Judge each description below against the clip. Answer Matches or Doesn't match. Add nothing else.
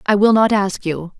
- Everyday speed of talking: Doesn't match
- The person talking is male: Doesn't match